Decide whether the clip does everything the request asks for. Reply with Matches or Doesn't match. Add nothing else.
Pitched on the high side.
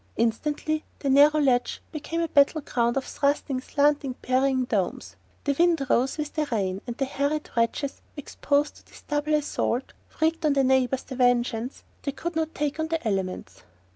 Matches